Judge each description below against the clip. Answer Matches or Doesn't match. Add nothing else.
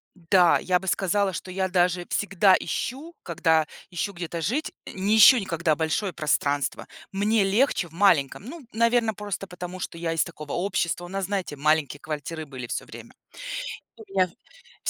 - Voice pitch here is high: Doesn't match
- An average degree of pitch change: Matches